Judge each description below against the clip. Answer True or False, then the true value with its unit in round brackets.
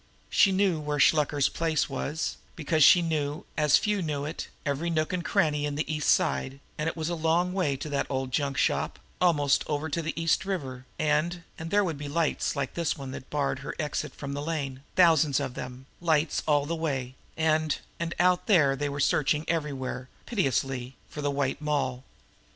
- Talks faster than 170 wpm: True (200 wpm)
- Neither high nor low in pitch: True (150 Hz)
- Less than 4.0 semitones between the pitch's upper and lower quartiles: True (2.8 semitones)